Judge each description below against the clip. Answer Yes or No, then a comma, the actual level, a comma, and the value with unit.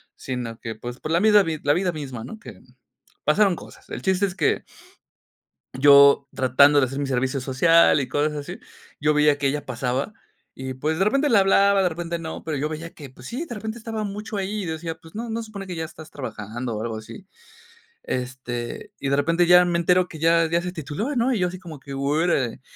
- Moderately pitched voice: Yes, medium, 160 Hz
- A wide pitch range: Yes, wide, 5.7 semitones